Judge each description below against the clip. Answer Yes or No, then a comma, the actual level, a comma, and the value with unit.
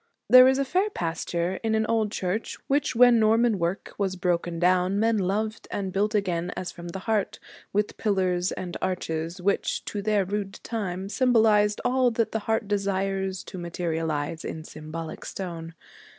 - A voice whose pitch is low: No, high, 195 Hz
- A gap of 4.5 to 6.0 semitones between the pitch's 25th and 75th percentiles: No, average, 3.8 semitones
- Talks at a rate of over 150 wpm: Yes, average, 165 wpm